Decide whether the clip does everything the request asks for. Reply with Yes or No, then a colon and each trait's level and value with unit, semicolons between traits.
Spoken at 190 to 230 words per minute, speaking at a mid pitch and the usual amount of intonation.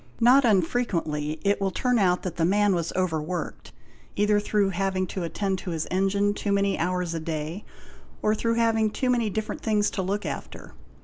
No: average, 195 wpm; high, 195 Hz; average, 3.2 semitones